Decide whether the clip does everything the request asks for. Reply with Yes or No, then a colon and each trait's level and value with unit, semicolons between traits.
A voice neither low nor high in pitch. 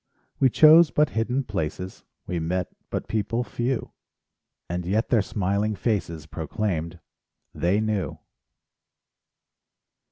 No: low, 105 Hz